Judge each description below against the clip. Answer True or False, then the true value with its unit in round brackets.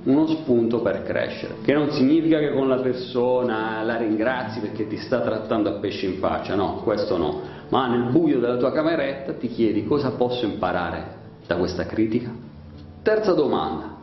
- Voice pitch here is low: True (120 Hz)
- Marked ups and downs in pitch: True (6.7 semitones)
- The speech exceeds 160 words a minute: True (170 wpm)